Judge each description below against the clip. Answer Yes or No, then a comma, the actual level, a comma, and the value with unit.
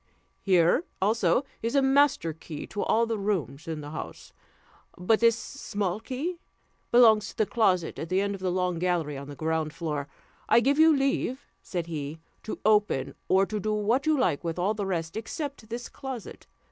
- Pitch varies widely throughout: Yes, wide, 5.9 semitones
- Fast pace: No, average, 190 wpm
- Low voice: No, high, 200 Hz